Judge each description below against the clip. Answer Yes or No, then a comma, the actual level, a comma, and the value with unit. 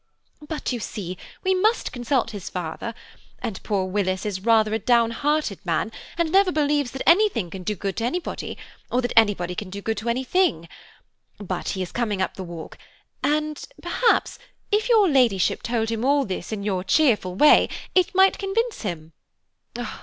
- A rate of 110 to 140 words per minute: No, average, 175 wpm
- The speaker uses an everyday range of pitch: No, wide, 7.7 semitones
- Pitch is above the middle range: Yes, high, 230 Hz